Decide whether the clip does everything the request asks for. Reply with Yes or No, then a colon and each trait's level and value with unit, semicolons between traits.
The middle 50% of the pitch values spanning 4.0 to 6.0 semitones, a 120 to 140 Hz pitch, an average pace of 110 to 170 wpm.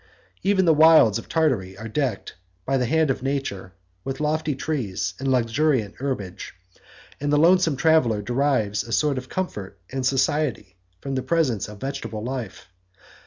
Yes: wide, 5.5 semitones; low, 135 Hz; average, 160 wpm